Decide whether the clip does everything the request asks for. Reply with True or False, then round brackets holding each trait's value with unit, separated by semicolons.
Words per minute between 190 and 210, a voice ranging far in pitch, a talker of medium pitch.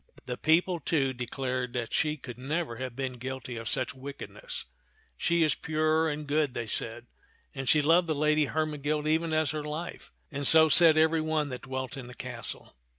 False (195 wpm; 3.5 semitones; 150 Hz)